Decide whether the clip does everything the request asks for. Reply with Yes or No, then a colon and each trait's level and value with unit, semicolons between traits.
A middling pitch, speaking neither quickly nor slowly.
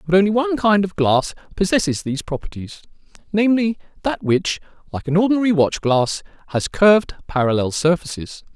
Yes: medium, 180 Hz; average, 145 wpm